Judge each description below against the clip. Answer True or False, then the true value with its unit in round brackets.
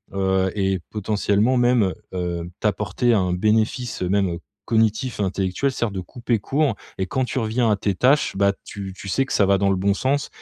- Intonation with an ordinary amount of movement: True (4.2 semitones)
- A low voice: True (105 Hz)